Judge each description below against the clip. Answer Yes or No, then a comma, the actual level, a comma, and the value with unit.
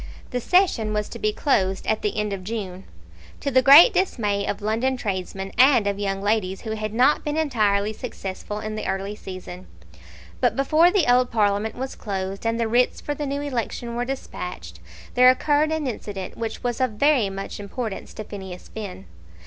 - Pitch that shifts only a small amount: No, average, 4.4 semitones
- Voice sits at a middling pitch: No, high, 220 Hz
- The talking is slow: No, average, 190 wpm